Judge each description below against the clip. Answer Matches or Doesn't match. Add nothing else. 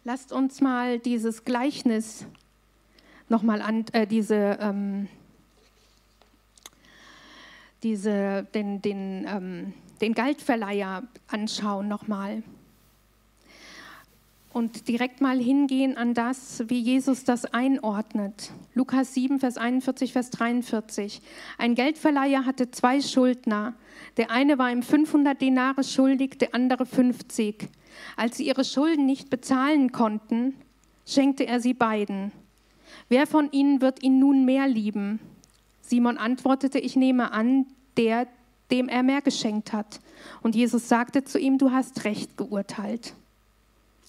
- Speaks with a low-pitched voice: Doesn't match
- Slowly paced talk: Matches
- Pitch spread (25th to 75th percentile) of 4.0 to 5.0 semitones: Doesn't match